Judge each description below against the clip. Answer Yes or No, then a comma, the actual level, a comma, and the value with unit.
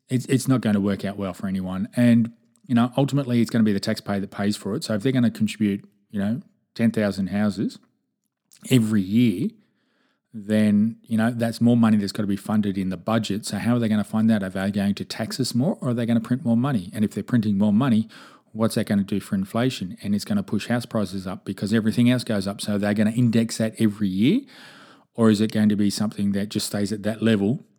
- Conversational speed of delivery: No, fast, 260 wpm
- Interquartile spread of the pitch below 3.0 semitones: Yes, narrow, 2.6 semitones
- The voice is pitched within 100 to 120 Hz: Yes, low, 110 Hz